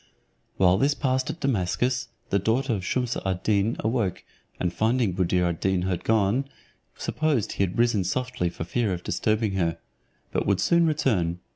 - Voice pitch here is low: Yes, low, 105 Hz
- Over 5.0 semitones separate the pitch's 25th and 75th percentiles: Yes, wide, 5.5 semitones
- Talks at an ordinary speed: Yes, average, 165 wpm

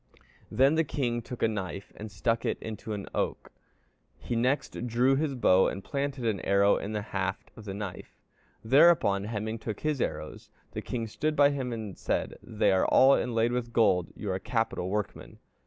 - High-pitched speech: No, low, 115 Hz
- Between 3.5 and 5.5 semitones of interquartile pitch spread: Yes, average, 4.2 semitones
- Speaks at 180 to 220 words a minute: Yes, average, 190 wpm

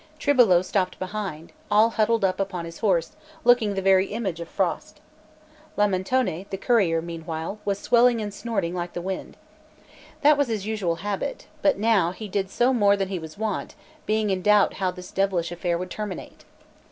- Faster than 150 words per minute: Yes, average, 175 wpm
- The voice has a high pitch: Yes, high, 195 Hz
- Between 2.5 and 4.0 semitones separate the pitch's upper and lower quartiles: Yes, average, 3.3 semitones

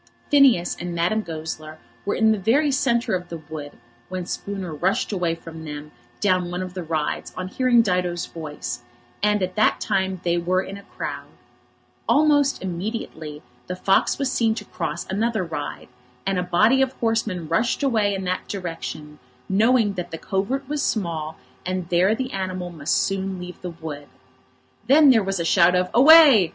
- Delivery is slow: No, average, 175 wpm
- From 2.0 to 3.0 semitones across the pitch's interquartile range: No, average, 4.4 semitones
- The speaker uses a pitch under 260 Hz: Yes, medium, 185 Hz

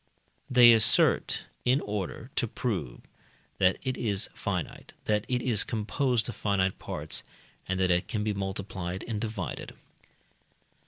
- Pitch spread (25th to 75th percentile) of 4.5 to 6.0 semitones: No, average, 3.8 semitones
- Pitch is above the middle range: No, low, 105 Hz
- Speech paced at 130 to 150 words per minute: Yes, average, 140 wpm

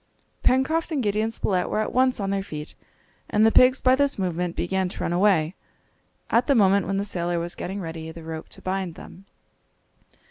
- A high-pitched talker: Yes, high, 195 Hz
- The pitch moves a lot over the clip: No, average, 4.3 semitones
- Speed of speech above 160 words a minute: Yes, average, 200 wpm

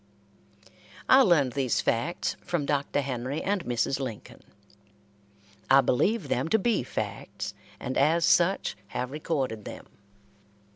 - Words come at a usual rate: No, slow, 125 wpm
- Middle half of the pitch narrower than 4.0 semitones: No, average, 5.1 semitones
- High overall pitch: No, medium, 140 Hz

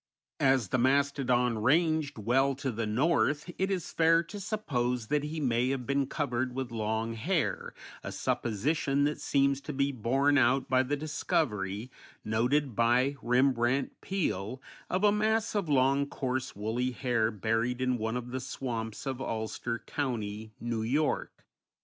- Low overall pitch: Yes, low, 130 Hz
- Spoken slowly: No, average, 155 wpm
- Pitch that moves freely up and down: No, average, 3.6 semitones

